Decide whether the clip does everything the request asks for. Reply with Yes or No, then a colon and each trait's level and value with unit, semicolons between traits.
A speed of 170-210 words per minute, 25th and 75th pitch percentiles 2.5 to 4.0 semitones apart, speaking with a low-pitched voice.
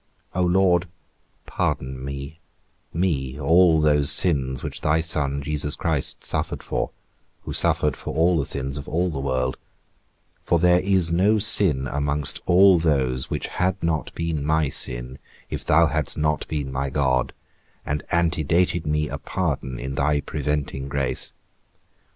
No: average, 150 wpm; average, 3.7 semitones; very low, 75 Hz